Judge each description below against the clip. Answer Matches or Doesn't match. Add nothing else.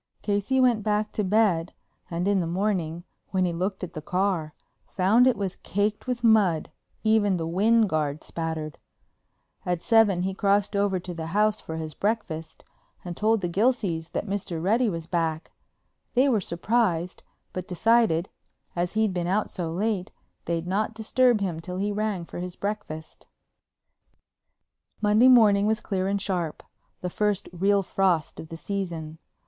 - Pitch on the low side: Doesn't match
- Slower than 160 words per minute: Doesn't match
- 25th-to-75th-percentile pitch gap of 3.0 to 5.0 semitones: Matches